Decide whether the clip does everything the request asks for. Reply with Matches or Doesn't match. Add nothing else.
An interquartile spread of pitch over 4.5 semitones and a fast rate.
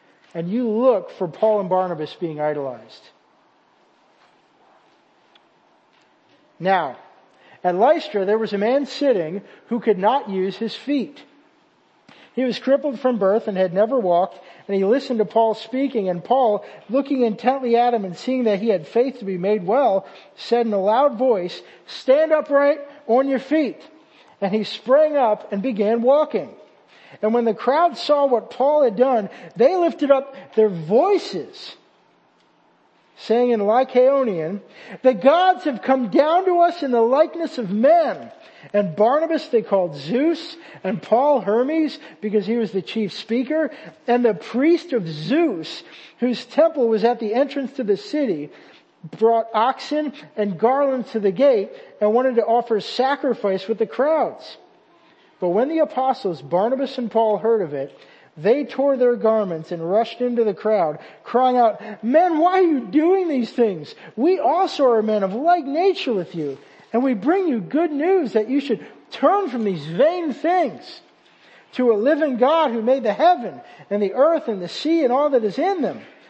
Doesn't match